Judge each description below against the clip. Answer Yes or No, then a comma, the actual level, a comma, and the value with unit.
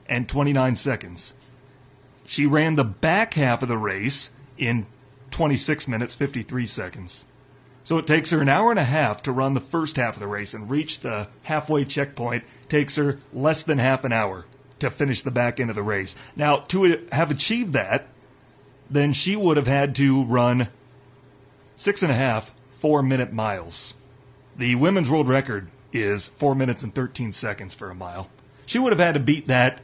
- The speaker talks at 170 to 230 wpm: Yes, average, 190 wpm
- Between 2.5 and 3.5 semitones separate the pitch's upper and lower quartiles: Yes, average, 3.0 semitones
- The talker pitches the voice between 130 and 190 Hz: Yes, low, 135 Hz